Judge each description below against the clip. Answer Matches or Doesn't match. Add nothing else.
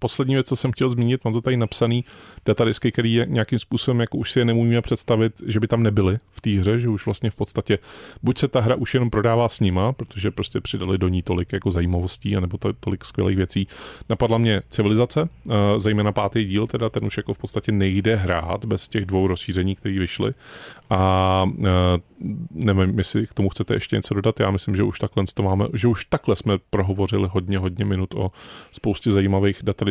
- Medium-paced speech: Doesn't match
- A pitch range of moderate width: Matches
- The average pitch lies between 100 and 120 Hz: Matches